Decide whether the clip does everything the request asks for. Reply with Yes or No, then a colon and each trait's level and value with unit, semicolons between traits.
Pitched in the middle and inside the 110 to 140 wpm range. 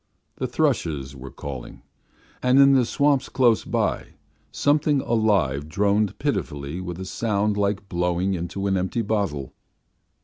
No: low, 100 Hz; slow, 135 wpm